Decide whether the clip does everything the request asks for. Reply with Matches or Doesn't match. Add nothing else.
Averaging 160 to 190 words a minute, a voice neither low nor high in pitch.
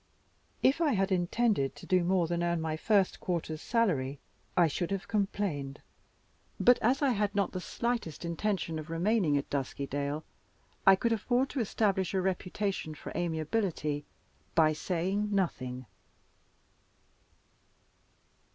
Doesn't match